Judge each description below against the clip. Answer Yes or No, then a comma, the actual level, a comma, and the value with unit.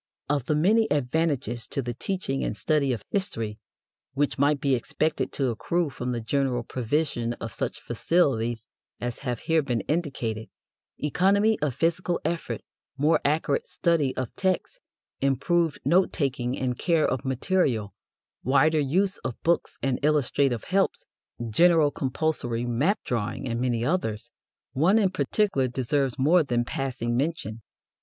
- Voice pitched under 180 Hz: Yes, medium, 140 Hz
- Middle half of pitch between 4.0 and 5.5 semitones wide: Yes, average, 5.2 semitones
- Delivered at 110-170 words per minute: Yes, average, 145 wpm